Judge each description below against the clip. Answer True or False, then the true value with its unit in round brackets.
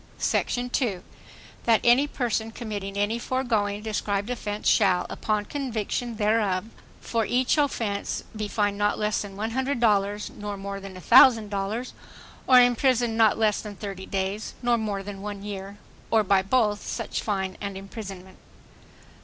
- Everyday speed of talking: True (145 wpm)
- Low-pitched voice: False (210 Hz)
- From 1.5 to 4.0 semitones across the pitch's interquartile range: True (2.6 semitones)